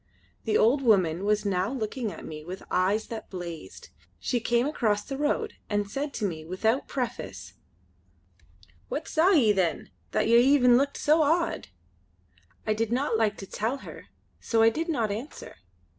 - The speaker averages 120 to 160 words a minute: No, average, 170 wpm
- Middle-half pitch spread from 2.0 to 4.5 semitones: No, average, 5.1 semitones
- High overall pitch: Yes, high, 225 Hz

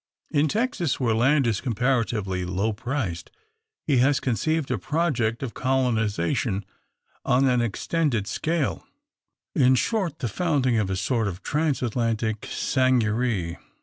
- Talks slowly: Yes, slow, 120 wpm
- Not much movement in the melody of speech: No, average, 4.4 semitones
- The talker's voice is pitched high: No, low, 125 Hz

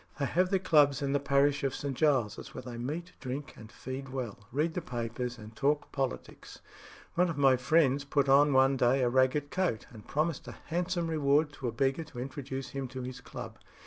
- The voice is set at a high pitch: No, low, 135 Hz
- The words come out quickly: Yes, fast, 210 wpm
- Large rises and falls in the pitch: No, average, 2.7 semitones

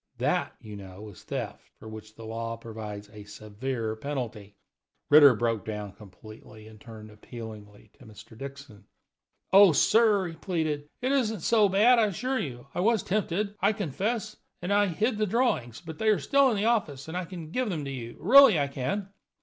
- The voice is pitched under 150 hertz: Yes, medium, 140 Hz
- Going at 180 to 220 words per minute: Yes, average, 185 wpm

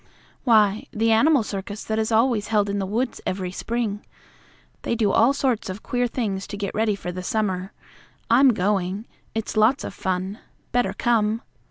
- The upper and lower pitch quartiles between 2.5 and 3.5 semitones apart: Yes, average, 2.8 semitones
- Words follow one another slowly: No, average, 175 wpm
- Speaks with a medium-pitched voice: No, high, 215 Hz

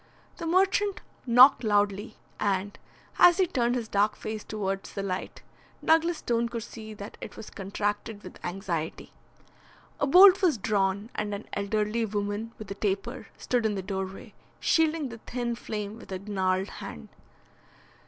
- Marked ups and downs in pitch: No, average, 3.4 semitones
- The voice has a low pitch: No, high, 215 Hz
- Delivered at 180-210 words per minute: No, average, 155 wpm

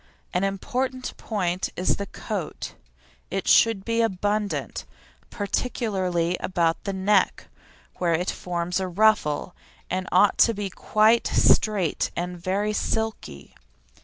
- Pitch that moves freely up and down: No, average, 3.1 semitones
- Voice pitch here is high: Yes, high, 195 Hz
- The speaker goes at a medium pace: No, slow, 125 wpm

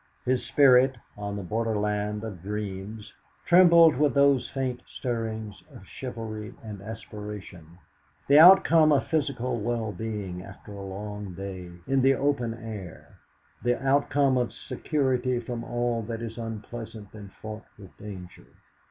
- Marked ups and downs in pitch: No, average, 3.9 semitones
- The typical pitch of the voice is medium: No, low, 115 Hz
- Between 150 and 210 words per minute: No, slow, 135 wpm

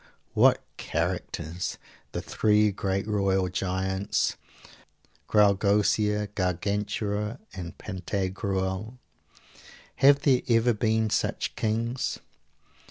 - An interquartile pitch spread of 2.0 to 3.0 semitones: Yes, narrow, 2.4 semitones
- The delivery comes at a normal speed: No, slow, 80 wpm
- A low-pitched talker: Yes, low, 105 Hz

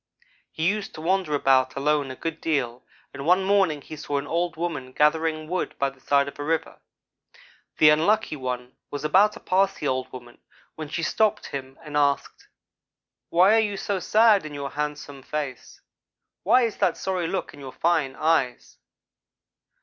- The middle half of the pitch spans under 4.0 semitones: No, average, 4.7 semitones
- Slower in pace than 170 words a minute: No, average, 180 wpm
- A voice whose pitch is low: No, medium, 155 Hz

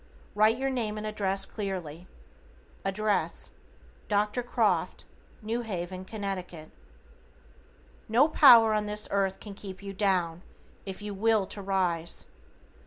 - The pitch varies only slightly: Yes, narrow, 2.3 semitones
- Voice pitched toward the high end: Yes, high, 200 Hz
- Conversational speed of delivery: No, slow, 120 wpm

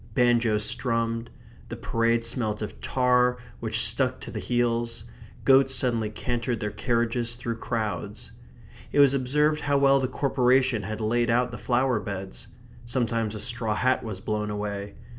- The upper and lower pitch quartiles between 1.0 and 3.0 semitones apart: Yes, narrow, 2.6 semitones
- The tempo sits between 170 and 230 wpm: No, average, 155 wpm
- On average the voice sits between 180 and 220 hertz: No, low, 120 Hz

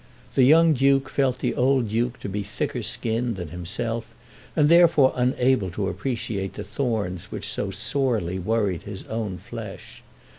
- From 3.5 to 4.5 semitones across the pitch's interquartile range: No, average, 5.0 semitones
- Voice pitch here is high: No, low, 115 Hz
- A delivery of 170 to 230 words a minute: No, average, 155 wpm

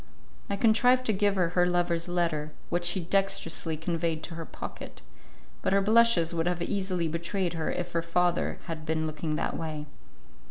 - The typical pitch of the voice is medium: Yes, medium, 175 Hz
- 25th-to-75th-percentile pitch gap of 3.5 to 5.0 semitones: No, narrow, 2.5 semitones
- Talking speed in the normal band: Yes, average, 175 wpm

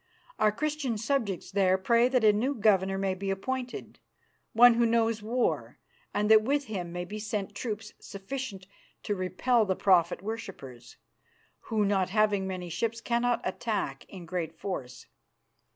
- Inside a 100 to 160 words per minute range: Yes, average, 150 wpm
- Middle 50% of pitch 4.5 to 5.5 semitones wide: No, average, 3.7 semitones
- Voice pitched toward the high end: Yes, high, 210 Hz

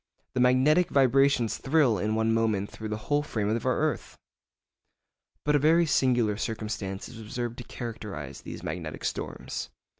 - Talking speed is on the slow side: No, average, 155 wpm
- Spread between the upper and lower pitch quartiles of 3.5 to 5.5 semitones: Yes, average, 4.2 semitones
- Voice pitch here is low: Yes, low, 120 Hz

